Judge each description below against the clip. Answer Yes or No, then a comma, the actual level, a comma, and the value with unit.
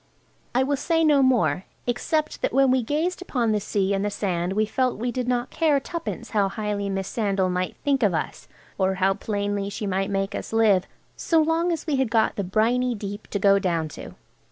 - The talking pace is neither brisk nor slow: No, fast, 215 wpm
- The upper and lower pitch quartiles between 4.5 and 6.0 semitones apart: Yes, average, 5.2 semitones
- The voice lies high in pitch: Yes, high, 215 Hz